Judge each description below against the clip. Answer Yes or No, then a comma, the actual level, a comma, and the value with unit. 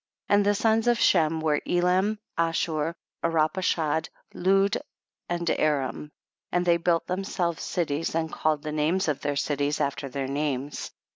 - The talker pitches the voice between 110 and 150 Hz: No, medium, 165 Hz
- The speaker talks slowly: No, average, 155 wpm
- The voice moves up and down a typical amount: Yes, average, 3.3 semitones